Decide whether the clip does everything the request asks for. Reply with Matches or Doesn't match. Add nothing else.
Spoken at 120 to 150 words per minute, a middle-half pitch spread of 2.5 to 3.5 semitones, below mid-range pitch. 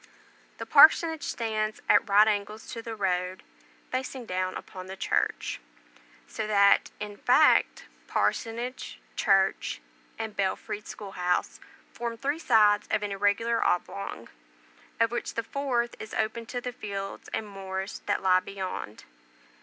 Doesn't match